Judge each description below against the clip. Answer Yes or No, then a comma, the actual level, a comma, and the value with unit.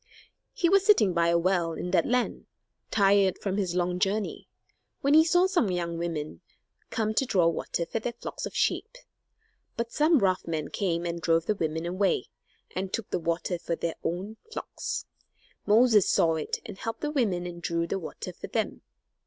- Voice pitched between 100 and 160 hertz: No, medium, 185 Hz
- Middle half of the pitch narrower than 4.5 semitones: No, average, 4.9 semitones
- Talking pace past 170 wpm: Yes, average, 185 wpm